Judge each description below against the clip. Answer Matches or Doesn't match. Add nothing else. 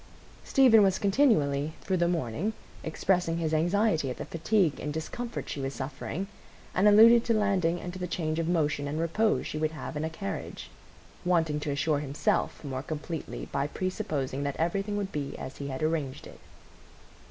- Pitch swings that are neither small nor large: Matches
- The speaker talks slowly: Doesn't match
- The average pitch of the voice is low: Doesn't match